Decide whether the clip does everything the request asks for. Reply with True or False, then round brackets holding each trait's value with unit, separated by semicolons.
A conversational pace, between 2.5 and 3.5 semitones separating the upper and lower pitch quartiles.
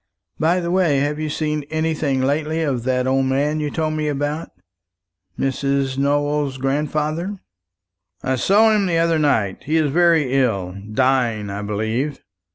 True (155 wpm; 3.1 semitones)